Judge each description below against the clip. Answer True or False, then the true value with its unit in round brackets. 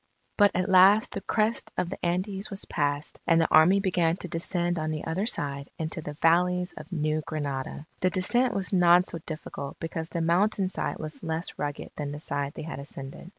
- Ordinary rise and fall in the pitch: True (3.2 semitones)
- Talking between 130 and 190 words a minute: False (200 wpm)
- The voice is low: False (170 Hz)